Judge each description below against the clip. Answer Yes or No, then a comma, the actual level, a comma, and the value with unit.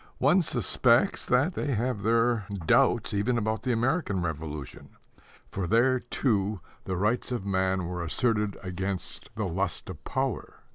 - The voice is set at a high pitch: No, low, 105 Hz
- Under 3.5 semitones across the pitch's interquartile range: No, average, 4.7 semitones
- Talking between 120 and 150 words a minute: Yes, average, 145 wpm